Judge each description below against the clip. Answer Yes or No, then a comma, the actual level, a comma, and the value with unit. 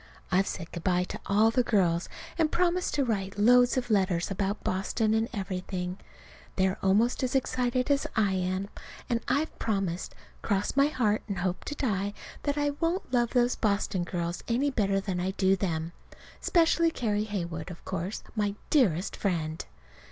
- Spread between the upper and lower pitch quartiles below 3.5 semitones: No, average, 4.9 semitones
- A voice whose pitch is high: Yes, high, 205 Hz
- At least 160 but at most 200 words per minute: Yes, average, 170 wpm